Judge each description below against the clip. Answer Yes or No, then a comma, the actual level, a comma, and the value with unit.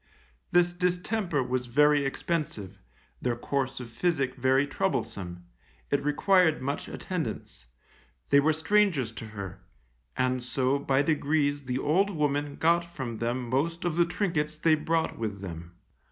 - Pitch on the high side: No, medium, 140 Hz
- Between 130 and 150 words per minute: Yes, average, 140 wpm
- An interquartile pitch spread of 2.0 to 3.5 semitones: No, average, 4.7 semitones